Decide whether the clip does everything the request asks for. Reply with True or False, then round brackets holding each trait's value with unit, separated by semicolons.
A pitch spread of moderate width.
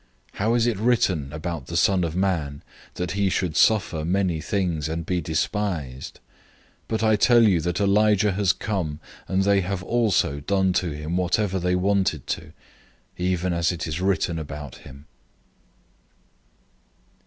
True (3.7 semitones)